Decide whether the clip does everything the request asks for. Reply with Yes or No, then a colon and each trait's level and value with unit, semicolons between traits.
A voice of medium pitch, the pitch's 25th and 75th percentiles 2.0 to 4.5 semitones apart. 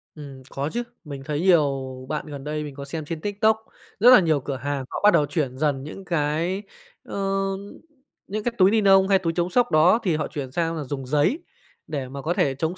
No: medium, 155 Hz; average, 5.1 semitones